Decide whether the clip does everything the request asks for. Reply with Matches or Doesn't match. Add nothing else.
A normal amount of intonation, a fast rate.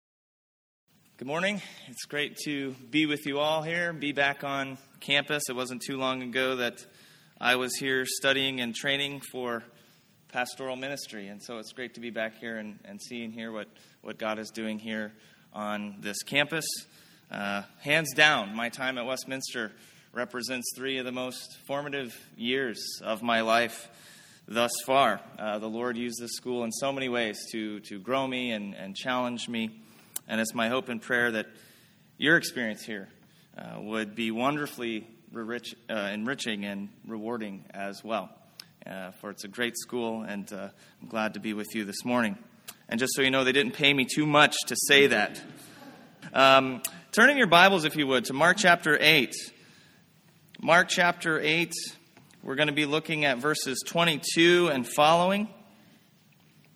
Doesn't match